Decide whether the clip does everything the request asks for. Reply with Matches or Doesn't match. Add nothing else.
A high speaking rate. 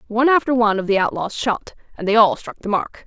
Matches